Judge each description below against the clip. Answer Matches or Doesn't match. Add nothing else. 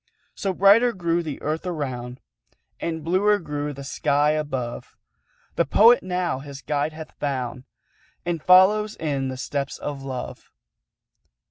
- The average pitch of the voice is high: Doesn't match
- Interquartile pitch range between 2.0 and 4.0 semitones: Doesn't match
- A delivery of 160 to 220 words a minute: Doesn't match